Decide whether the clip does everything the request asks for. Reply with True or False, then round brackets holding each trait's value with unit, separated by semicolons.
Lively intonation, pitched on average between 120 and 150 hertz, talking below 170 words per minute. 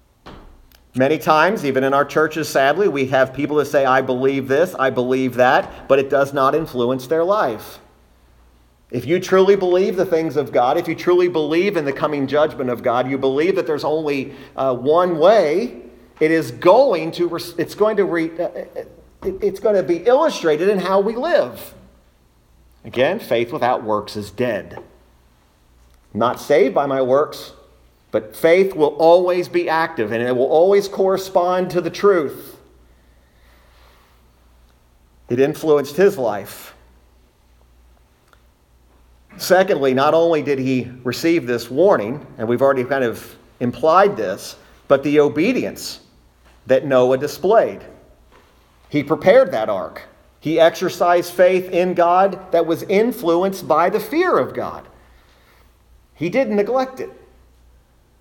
True (8.8 semitones; 140 Hz; 140 wpm)